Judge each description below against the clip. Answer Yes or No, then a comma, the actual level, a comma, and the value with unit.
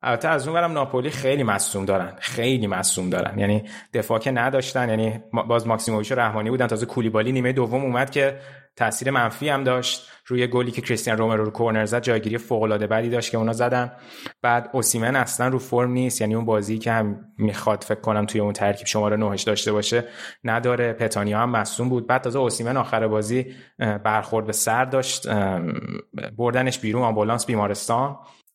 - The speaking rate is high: Yes, fast, 180 wpm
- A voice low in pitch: Yes, low, 115 Hz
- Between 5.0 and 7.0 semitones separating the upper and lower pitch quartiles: No, average, 2.7 semitones